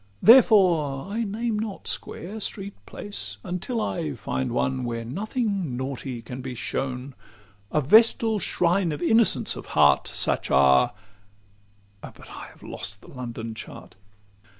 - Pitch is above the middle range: No, medium, 150 Hz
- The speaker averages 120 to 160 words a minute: Yes, slow, 135 wpm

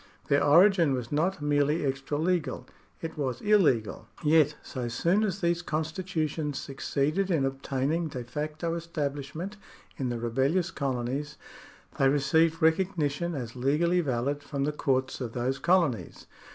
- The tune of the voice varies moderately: Yes, average, 3.8 semitones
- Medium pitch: Yes, medium, 150 Hz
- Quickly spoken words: No, average, 140 wpm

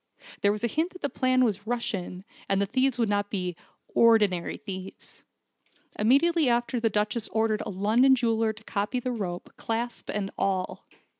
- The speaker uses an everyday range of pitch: Yes, average, 3.3 semitones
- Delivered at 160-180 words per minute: Yes, average, 170 wpm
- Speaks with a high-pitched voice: Yes, high, 220 Hz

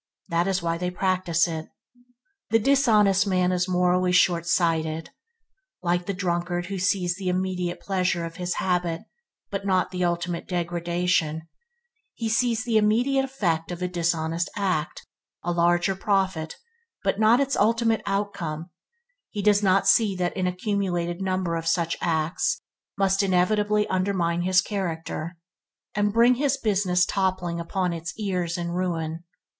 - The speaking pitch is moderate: Yes, medium, 180 Hz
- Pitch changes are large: No, narrow, 2.6 semitones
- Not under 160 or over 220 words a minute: No, average, 150 wpm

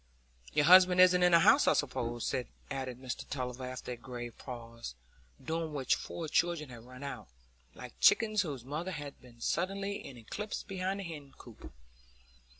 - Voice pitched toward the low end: No, medium, 145 Hz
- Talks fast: No, average, 165 wpm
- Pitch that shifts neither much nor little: No, wide, 6.1 semitones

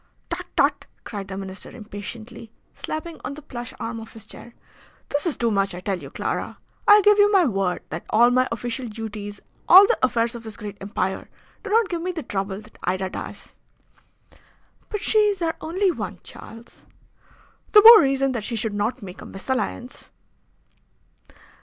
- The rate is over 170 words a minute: Yes, average, 180 wpm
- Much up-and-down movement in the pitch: Yes, wide, 7.9 semitones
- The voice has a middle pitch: No, high, 235 Hz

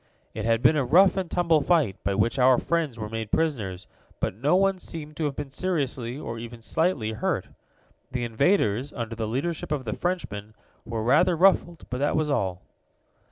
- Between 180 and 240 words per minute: Yes, average, 190 wpm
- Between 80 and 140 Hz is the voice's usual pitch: Yes, low, 135 Hz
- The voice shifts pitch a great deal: Yes, wide, 6.4 semitones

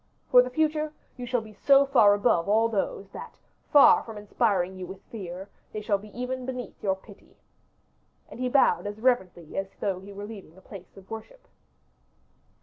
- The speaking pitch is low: No, high, 215 Hz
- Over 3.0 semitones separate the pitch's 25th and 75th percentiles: Yes, average, 4.4 semitones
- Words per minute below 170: No, average, 185 wpm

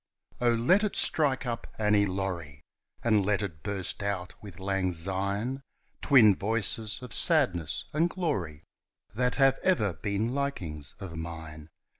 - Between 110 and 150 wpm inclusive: Yes, average, 140 wpm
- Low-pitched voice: Yes, low, 100 Hz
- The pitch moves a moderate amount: No, wide, 5.8 semitones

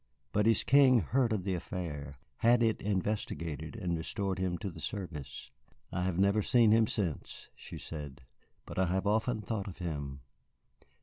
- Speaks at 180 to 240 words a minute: No, average, 170 wpm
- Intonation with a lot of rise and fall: No, average, 4.6 semitones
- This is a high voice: No, very low, 95 Hz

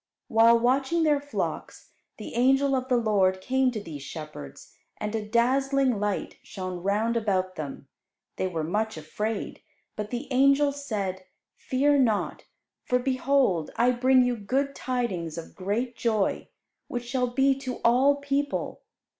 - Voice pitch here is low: No, high, 235 Hz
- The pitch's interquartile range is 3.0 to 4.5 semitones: No, average, 4.9 semitones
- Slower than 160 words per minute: Yes, average, 145 wpm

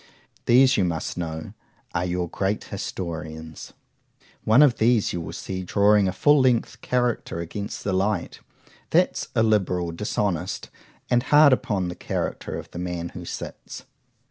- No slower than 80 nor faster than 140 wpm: Yes, slow, 135 wpm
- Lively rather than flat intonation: No, average, 4.4 semitones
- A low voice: Yes, very low, 95 Hz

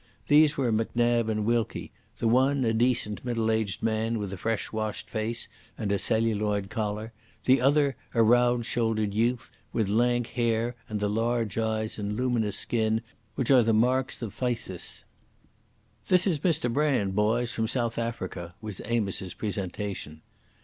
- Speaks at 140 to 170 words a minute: Yes, average, 155 wpm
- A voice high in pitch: No, low, 115 Hz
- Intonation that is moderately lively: No, narrow, 2.2 semitones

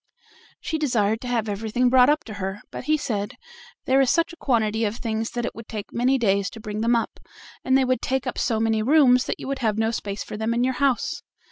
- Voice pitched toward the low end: No, high, 235 Hz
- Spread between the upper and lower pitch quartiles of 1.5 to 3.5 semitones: Yes, average, 3.1 semitones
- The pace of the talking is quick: Yes, fast, 250 wpm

